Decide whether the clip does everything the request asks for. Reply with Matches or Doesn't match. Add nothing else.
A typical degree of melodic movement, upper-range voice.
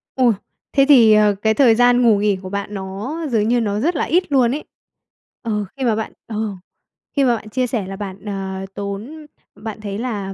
Matches